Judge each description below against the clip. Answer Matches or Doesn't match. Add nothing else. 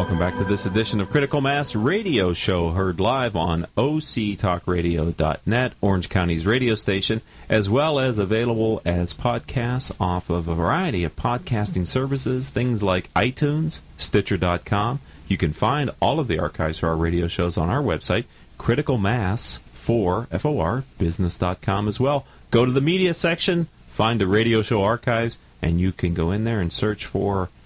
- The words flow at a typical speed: Matches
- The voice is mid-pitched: Doesn't match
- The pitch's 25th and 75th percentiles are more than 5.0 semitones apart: Matches